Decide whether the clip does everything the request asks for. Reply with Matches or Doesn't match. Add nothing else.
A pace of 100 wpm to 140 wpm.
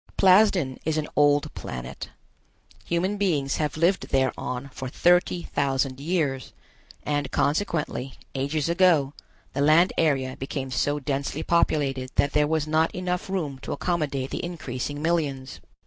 Matches